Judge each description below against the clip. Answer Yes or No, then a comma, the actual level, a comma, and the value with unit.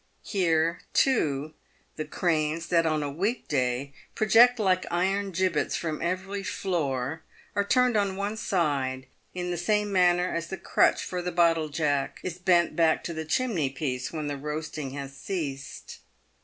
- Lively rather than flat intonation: No, average, 4.0 semitones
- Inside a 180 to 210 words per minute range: No, average, 165 wpm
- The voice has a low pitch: No, medium, 170 Hz